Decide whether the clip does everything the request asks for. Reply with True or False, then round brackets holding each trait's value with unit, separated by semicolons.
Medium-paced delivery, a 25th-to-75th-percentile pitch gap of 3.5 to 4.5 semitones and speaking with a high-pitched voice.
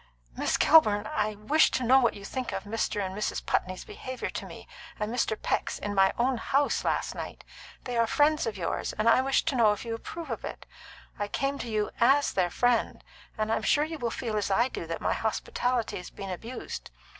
False (225 wpm; 3.9 semitones; 225 Hz)